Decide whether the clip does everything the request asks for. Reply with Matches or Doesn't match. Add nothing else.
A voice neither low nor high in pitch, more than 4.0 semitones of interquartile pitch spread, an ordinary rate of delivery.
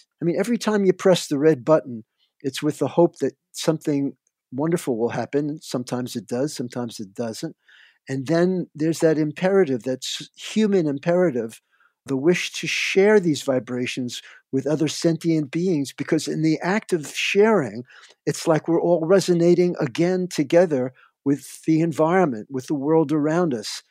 Matches